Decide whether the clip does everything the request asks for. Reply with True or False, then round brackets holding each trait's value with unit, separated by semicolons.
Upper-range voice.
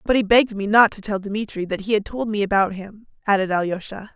True (205 Hz)